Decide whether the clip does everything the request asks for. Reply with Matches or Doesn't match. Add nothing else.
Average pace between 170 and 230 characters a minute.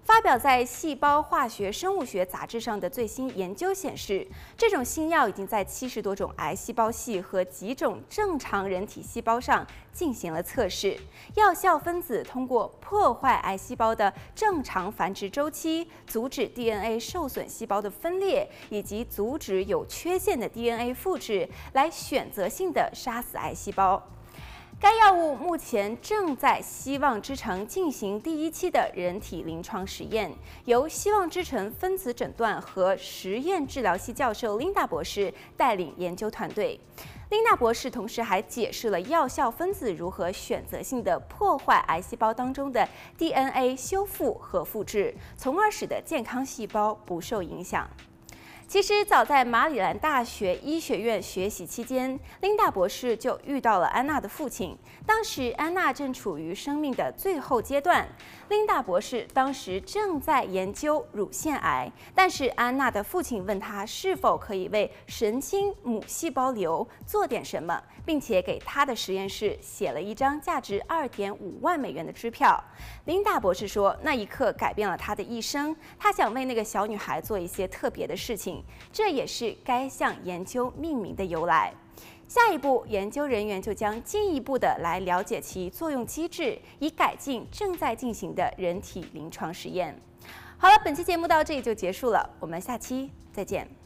Doesn't match